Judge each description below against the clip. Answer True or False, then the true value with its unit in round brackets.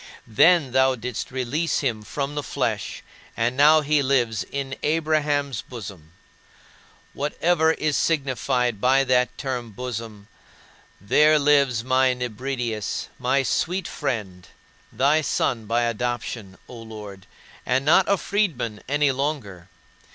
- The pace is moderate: False (120 wpm)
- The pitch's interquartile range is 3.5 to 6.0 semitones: True (4.2 semitones)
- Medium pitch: False (130 Hz)